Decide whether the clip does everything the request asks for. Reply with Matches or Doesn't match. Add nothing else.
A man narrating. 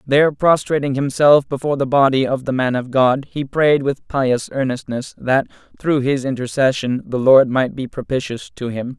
Matches